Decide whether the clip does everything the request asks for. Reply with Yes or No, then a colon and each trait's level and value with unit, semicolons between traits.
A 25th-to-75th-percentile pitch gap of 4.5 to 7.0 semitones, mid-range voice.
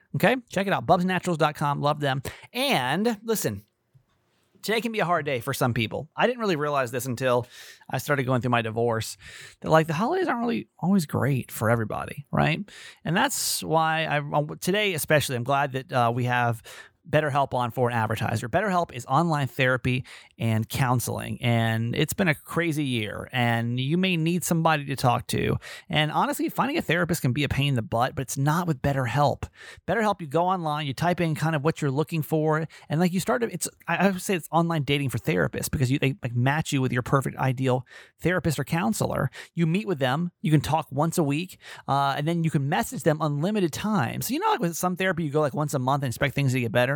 Yes: average, 5.1 semitones; medium, 150 Hz